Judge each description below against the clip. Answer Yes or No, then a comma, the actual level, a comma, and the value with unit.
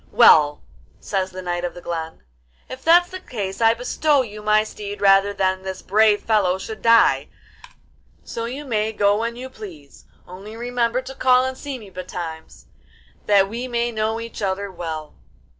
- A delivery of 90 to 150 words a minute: No, average, 175 wpm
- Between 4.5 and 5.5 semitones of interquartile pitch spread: No, average, 3.9 semitones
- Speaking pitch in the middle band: No, high, 210 Hz